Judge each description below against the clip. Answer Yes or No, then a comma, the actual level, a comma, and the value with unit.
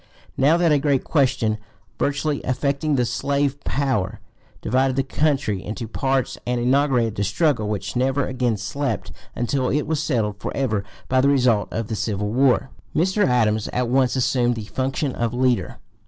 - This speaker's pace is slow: No, average, 170 wpm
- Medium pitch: No, low, 130 Hz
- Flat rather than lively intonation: No, average, 3.6 semitones